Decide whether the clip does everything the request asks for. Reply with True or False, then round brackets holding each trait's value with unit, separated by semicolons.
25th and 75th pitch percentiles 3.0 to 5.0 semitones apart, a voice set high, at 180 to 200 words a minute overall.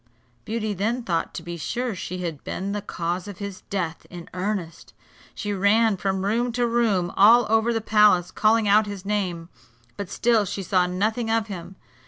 True (3.5 semitones; 200 Hz; 185 wpm)